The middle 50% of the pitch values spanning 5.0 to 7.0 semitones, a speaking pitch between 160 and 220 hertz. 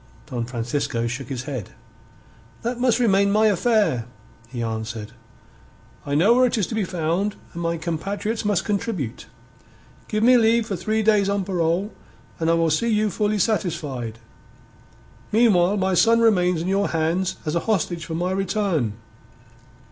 Yes: average, 5.3 semitones; medium, 185 Hz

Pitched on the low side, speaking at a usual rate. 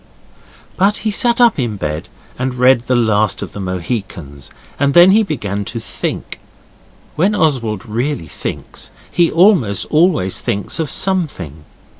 Yes: low, 125 Hz; average, 145 wpm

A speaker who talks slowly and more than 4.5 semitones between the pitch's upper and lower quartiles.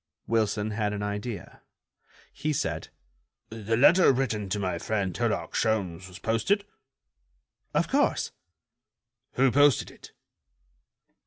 No: slow, 110 wpm; average, 3.6 semitones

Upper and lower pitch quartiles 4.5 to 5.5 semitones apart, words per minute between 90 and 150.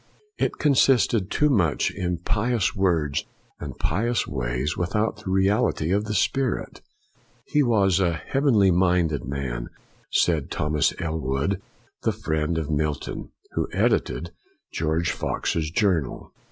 Yes: average, 5.2 semitones; average, 140 wpm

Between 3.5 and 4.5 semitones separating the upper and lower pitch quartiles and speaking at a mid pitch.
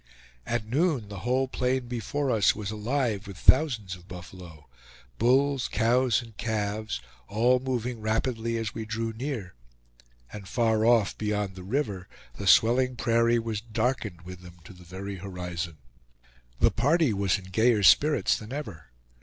No: average, 4.1 semitones; low, 110 Hz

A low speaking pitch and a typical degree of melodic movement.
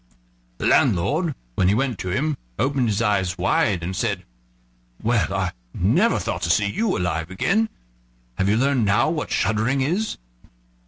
No: low, 110 Hz; wide, 6.6 semitones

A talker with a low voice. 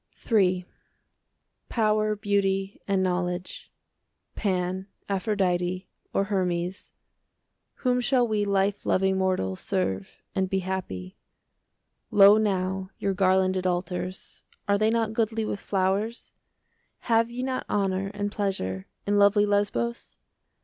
No: high, 195 Hz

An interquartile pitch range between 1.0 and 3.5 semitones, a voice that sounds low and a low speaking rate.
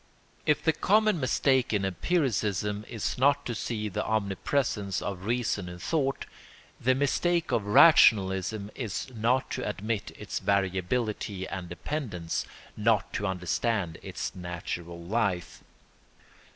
No: average, 5.3 semitones; low, 105 Hz; slow, 125 wpm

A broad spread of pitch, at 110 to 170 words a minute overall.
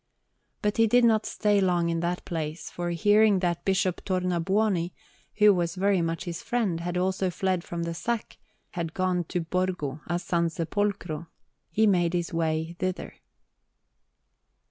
No: narrow, 2.6 semitones; average, 160 wpm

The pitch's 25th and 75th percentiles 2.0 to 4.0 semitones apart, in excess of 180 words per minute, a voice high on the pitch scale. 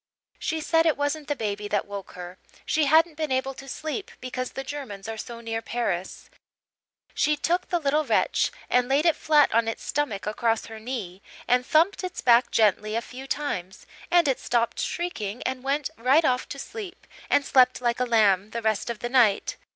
No: average, 4.9 semitones; average, 195 wpm; very high, 255 Hz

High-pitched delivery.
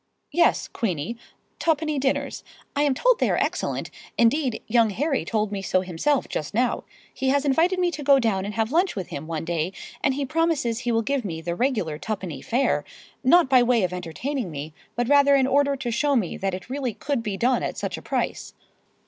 Yes: high, 245 Hz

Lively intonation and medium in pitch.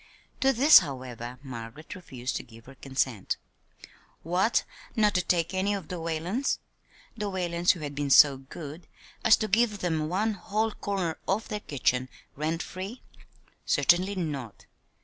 Yes: wide, 6.4 semitones; medium, 170 Hz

